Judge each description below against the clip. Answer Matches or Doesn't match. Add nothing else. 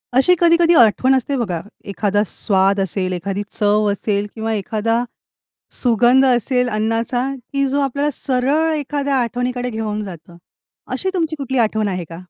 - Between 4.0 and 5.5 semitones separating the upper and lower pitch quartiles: Matches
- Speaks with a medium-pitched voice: Doesn't match